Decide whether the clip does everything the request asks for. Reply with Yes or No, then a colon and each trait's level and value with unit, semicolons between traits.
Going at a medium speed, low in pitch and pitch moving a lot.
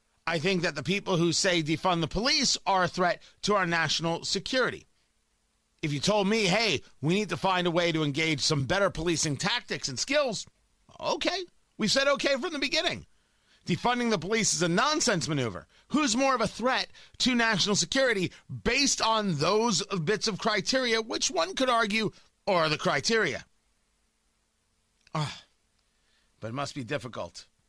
No: average, 165 wpm; high, 190 Hz; wide, 5.9 semitones